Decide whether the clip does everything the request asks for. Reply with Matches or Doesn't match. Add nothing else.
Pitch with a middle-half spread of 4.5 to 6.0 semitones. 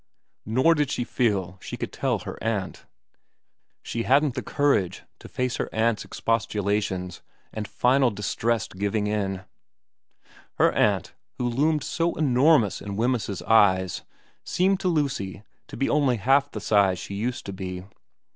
Matches